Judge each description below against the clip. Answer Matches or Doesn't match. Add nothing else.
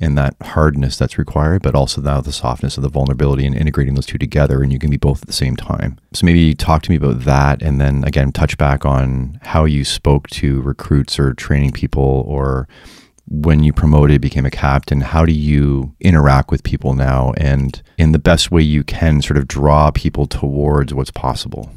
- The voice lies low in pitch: Matches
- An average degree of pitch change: Doesn't match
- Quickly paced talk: Matches